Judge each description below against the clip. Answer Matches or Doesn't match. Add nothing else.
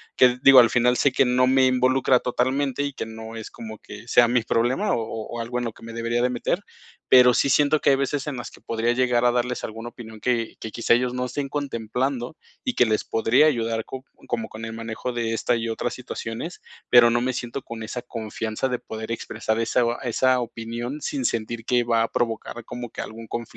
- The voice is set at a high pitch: Doesn't match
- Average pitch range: Doesn't match